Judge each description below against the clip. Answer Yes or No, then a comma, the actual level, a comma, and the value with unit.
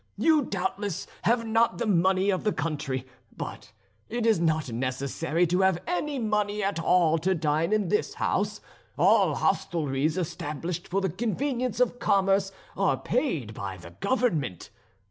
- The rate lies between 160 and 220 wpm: No, average, 150 wpm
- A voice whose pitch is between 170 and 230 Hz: Yes, high, 190 Hz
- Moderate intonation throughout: No, wide, 5.9 semitones